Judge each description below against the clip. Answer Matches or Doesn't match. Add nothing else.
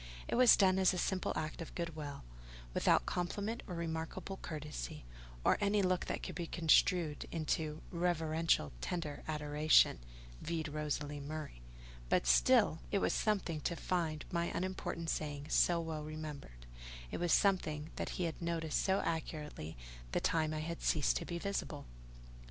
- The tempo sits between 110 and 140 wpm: Doesn't match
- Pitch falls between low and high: Matches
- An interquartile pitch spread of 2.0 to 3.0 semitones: Matches